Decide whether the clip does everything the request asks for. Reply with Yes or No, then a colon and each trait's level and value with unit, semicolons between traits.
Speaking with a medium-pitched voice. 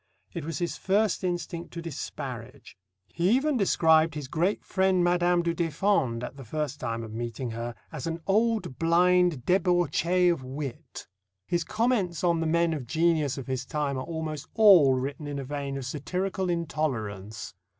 Yes: medium, 160 Hz